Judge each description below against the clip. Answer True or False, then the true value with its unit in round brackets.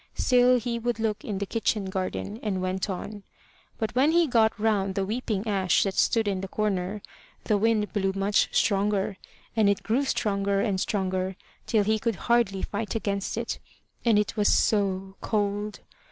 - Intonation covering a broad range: False (2.4 semitones)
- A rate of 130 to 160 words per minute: False (175 wpm)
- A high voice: True (205 Hz)